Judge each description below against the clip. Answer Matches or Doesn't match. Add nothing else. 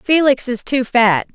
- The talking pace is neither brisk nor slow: Matches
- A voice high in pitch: Matches